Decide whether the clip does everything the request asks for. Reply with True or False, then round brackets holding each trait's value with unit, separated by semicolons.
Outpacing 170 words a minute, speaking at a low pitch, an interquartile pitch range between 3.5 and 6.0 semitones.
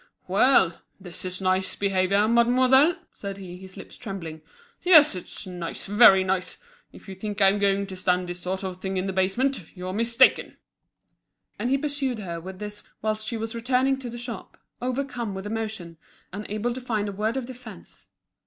False (180 wpm; 205 Hz; 4.3 semitones)